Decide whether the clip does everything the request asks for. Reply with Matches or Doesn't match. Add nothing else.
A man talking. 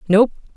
Doesn't match